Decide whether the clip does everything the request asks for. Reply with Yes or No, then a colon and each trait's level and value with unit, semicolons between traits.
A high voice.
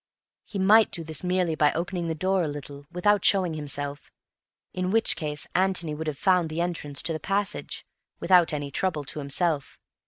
No: medium, 170 Hz